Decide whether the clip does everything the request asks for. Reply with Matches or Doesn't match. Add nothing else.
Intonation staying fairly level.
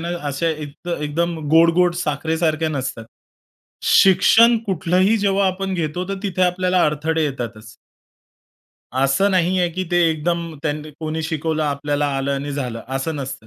Doesn't match